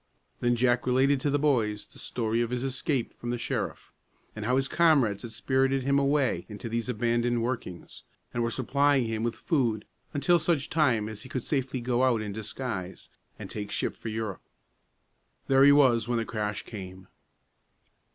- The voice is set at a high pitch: No, low, 120 Hz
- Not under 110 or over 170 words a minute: No, average, 180 wpm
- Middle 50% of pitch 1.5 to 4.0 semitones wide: Yes, average, 3.3 semitones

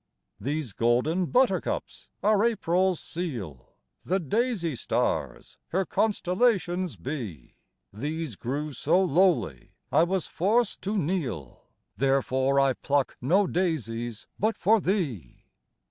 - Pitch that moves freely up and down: Yes, wide, 6.6 semitones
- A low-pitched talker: No, medium, 160 Hz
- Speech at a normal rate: No, slow, 110 wpm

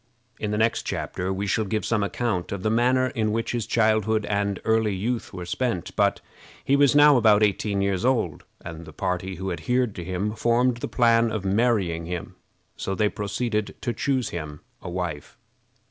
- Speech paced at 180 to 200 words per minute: Yes, average, 190 wpm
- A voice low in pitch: Yes, low, 105 Hz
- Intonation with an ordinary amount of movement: Yes, average, 3.8 semitones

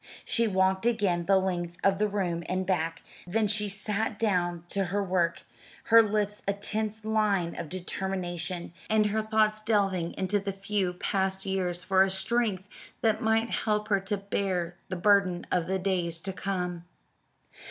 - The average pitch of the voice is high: Yes, high, 195 Hz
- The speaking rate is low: No, average, 165 wpm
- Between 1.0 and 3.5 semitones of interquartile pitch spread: Yes, average, 2.7 semitones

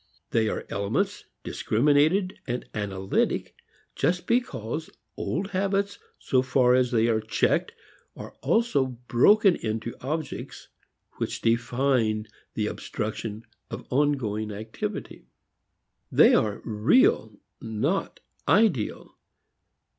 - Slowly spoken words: Yes, slow, 95 wpm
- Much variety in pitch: Yes, wide, 6.6 semitones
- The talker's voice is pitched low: Yes, low, 125 Hz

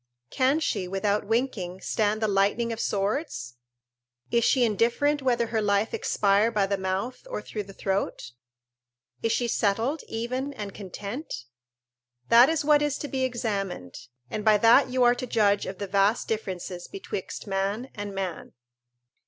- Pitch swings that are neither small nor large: Yes, average, 4.0 semitones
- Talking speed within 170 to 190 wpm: No, average, 160 wpm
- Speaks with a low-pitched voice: No, high, 215 Hz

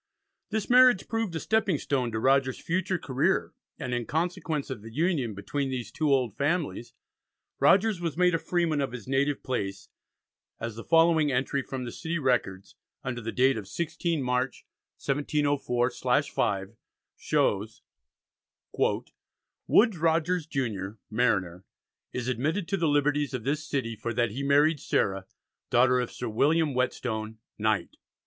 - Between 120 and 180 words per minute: Yes, average, 145 wpm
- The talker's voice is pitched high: No, low, 135 Hz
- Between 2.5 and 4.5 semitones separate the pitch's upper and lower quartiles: No, wide, 5.4 semitones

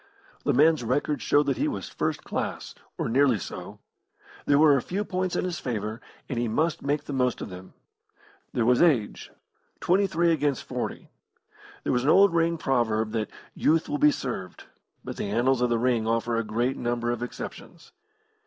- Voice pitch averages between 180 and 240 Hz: No, low, 130 Hz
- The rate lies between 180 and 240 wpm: Yes, average, 190 wpm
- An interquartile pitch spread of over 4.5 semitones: Yes, average, 5.3 semitones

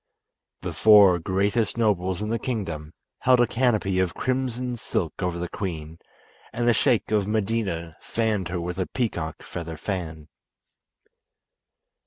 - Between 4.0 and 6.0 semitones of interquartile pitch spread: Yes, average, 4.8 semitones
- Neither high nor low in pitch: No, low, 100 Hz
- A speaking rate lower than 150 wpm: Yes, average, 140 wpm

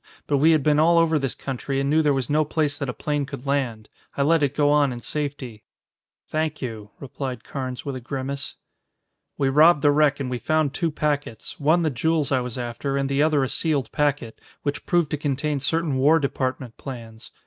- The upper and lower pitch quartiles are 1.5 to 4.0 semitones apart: Yes, narrow, 2.5 semitones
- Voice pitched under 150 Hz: Yes, medium, 140 Hz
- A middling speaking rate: No, fast, 215 wpm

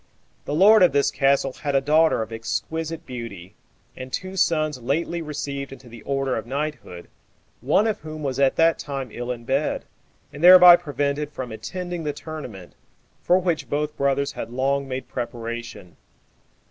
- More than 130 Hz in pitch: Yes, medium, 140 Hz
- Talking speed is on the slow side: No, average, 165 wpm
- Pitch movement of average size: Yes, average, 3.9 semitones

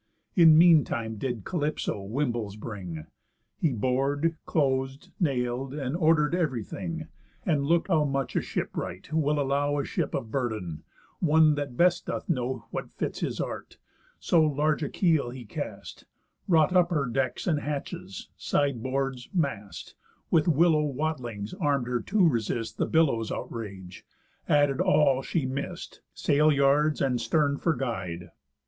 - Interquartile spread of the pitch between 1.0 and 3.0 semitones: No, average, 4.3 semitones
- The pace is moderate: Yes, average, 150 wpm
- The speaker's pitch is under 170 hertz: Yes, medium, 140 Hz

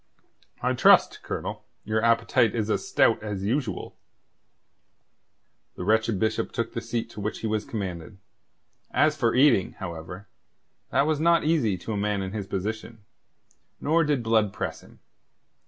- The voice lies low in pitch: Yes, low, 110 Hz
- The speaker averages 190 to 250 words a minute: No, average, 155 wpm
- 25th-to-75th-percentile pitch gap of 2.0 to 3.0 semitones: Yes, average, 2.7 semitones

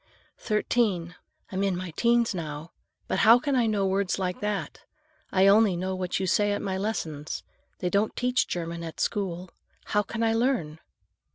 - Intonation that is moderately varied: Yes, average, 3.7 semitones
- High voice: Yes, high, 195 Hz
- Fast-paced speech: No, average, 175 wpm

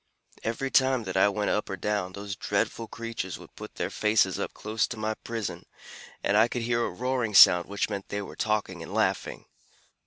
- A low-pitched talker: Yes, low, 105 Hz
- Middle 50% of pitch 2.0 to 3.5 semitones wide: Yes, narrow, 2.6 semitones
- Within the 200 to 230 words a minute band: Yes, fast, 205 wpm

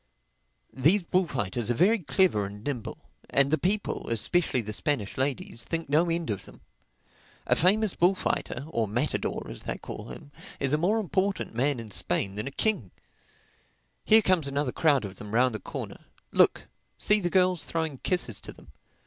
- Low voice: No, medium, 145 Hz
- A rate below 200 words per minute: Yes, average, 170 wpm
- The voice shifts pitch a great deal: Yes, wide, 7.7 semitones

